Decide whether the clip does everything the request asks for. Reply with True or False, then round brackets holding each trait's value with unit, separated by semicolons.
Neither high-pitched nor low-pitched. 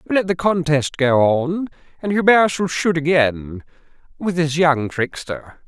True (160 Hz)